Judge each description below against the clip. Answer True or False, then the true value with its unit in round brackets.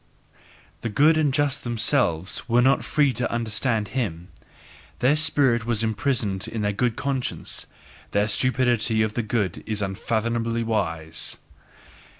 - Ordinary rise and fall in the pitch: True (3.7 semitones)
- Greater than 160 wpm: False (135 wpm)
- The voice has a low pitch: True (115 Hz)